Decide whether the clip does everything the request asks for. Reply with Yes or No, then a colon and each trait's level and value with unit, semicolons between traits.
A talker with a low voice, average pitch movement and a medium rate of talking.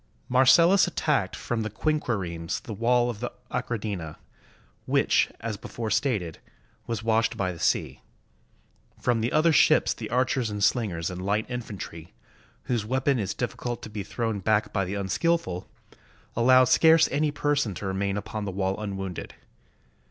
Yes: low, 110 Hz; average, 4.3 semitones; average, 150 wpm